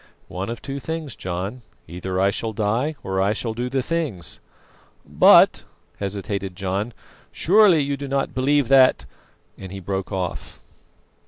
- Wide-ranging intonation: Yes, wide, 6.2 semitones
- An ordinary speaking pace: Yes, average, 155 wpm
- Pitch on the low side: Yes, low, 110 Hz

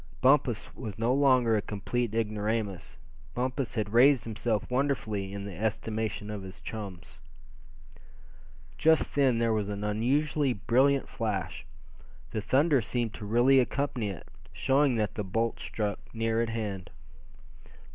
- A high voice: No, low, 115 Hz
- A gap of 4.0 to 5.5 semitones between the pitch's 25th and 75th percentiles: No, average, 3.6 semitones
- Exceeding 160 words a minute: No, slow, 135 wpm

